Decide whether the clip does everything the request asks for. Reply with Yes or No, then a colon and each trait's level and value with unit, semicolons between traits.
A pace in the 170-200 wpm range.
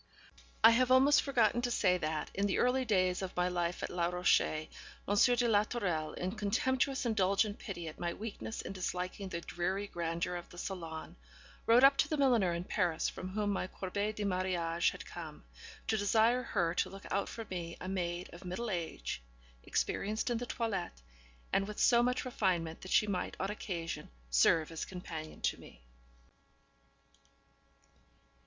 Yes: average, 175 wpm